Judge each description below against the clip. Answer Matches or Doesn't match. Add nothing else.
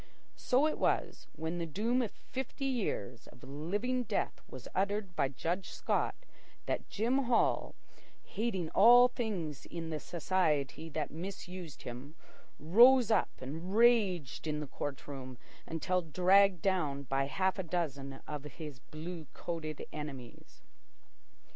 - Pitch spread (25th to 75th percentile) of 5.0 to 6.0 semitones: Matches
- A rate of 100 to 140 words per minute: Matches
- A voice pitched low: Doesn't match